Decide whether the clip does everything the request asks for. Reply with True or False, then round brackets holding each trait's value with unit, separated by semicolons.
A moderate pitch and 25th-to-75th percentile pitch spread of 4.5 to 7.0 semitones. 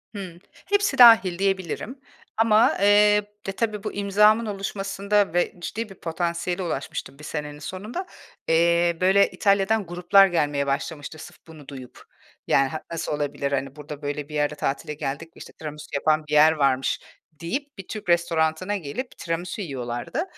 True (170 Hz; 5.0 semitones)